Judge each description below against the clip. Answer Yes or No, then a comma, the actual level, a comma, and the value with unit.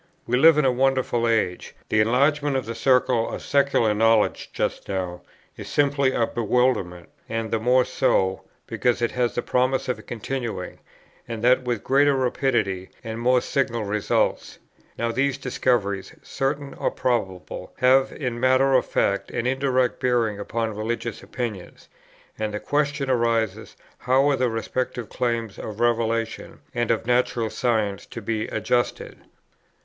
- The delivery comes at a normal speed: Yes, average, 150 wpm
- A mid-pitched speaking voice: No, low, 120 Hz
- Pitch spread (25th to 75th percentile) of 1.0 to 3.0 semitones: Yes, average, 2.7 semitones